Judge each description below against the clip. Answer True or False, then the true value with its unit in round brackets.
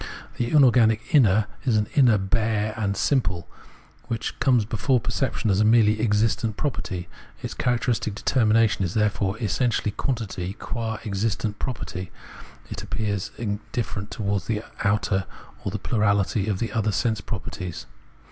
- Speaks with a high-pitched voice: False (110 Hz)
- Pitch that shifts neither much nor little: False (2.3 semitones)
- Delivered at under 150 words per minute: True (140 wpm)